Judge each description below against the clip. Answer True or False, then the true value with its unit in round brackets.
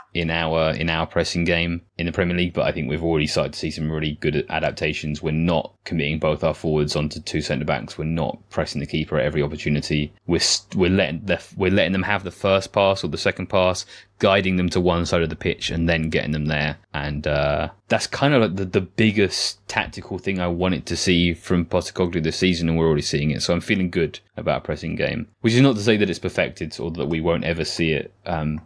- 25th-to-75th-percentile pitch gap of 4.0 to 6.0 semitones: False (3.0 semitones)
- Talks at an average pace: False (245 wpm)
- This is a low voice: True (85 Hz)